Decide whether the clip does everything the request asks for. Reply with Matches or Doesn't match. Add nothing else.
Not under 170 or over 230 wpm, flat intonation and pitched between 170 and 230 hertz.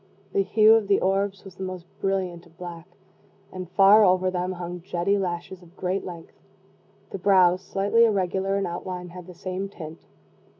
Matches